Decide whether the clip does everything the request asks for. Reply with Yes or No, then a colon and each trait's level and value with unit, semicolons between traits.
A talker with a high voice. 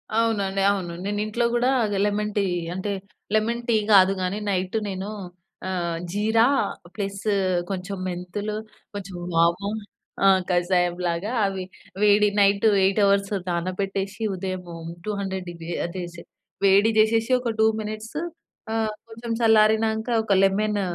Yes: high, 200 Hz